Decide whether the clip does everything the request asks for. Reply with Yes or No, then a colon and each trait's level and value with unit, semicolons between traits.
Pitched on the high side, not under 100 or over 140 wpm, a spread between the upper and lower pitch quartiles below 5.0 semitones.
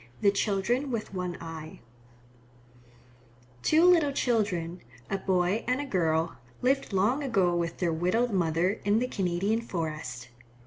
No: high, 195 Hz; slow, 135 wpm; wide, 5.5 semitones